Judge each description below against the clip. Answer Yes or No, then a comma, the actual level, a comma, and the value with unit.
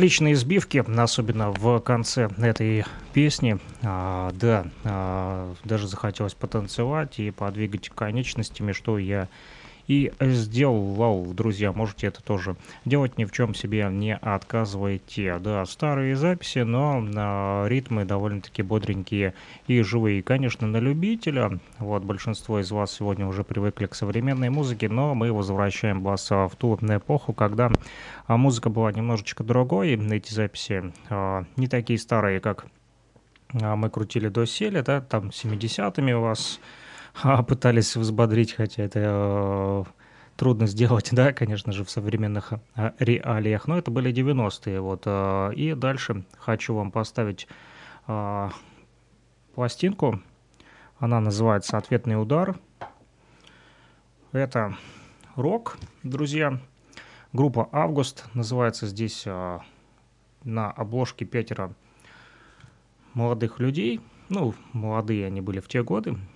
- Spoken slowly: No, average, 125 wpm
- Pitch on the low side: Yes, low, 110 Hz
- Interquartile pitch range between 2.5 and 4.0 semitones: Yes, average, 3.4 semitones